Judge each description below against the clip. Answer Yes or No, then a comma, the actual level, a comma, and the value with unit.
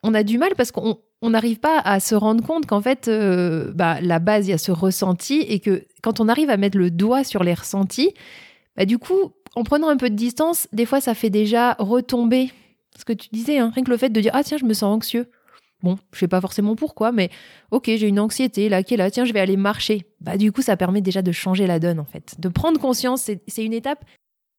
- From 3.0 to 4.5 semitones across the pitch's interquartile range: Yes, average, 4.2 semitones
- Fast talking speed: Yes, fast, 260 wpm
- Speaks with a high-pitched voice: Yes, high, 220 Hz